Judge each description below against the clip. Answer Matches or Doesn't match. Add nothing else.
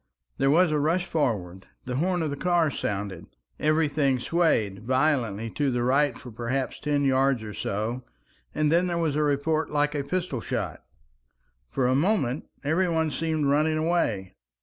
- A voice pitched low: Doesn't match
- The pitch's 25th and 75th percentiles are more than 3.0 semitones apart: Matches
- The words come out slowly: Doesn't match